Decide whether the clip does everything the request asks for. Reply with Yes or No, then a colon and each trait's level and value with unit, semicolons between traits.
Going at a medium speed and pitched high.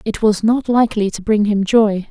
No: fast, 230 wpm; high, 215 Hz